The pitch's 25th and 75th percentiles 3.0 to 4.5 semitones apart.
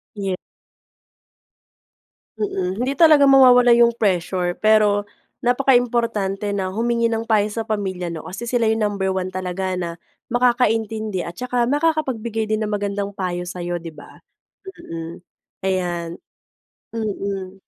Yes: average, 4.0 semitones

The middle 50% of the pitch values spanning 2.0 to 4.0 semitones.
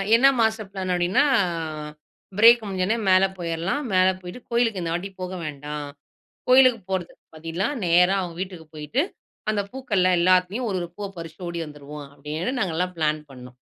Yes: average, 3.7 semitones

